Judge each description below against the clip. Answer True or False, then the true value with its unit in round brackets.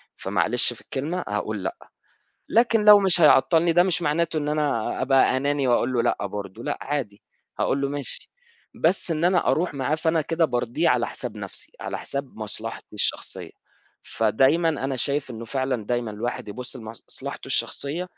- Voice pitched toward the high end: False (140 Hz)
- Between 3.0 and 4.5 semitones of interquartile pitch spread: False (5.5 semitones)